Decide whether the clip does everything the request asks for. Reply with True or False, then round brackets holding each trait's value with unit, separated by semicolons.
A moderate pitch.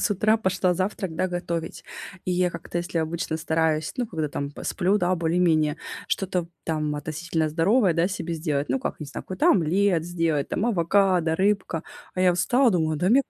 True (175 Hz)